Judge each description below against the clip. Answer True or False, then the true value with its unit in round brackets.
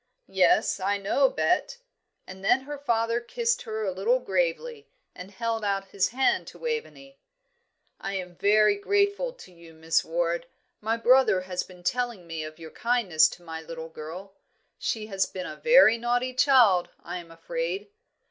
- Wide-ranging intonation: True (6.2 semitones)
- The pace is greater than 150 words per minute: True (165 wpm)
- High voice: True (205 Hz)